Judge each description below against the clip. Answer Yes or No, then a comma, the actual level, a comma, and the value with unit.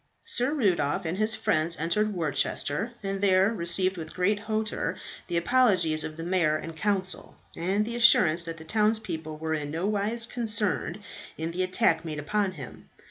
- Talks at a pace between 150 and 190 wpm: Yes, average, 165 wpm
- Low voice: No, medium, 185 Hz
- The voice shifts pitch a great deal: No, average, 4.6 semitones